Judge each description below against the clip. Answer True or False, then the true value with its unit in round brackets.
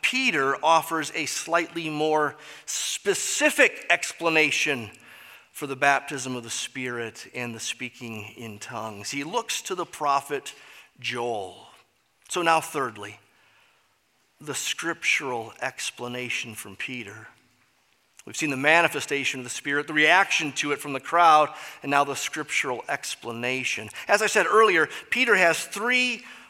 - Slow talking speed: True (130 wpm)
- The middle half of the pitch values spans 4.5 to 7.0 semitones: True (5.0 semitones)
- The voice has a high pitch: False (145 Hz)